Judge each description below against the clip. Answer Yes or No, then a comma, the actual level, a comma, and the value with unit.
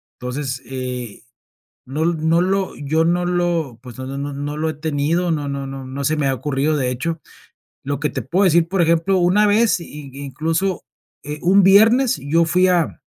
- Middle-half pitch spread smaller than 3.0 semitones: No, average, 4.2 semitones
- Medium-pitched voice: Yes, medium, 155 Hz